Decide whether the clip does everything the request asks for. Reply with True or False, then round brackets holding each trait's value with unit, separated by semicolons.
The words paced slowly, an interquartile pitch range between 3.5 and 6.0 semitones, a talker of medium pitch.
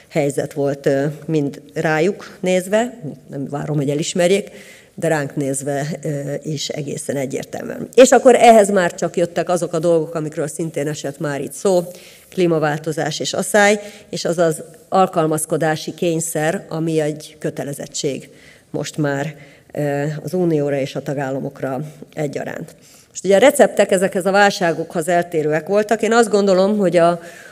False (135 wpm; 4.2 semitones; 165 Hz)